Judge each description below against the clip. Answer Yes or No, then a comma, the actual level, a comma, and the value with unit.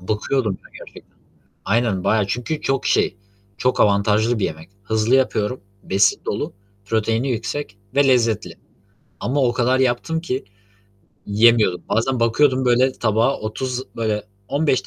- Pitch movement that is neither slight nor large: Yes, average, 3.4 semitones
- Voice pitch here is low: Yes, low, 115 Hz